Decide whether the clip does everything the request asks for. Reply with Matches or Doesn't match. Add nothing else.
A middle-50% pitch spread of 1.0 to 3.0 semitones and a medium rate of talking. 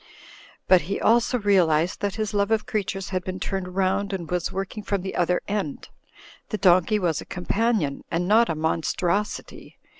Matches